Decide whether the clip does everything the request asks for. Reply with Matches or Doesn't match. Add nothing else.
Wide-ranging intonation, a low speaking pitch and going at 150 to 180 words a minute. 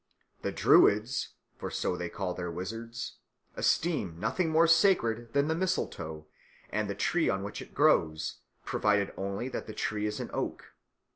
Matches